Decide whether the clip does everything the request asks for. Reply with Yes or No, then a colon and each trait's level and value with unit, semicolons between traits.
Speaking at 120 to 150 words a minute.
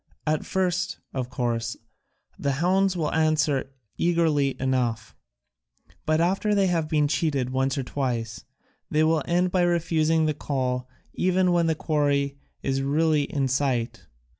Yes: average, 140 wpm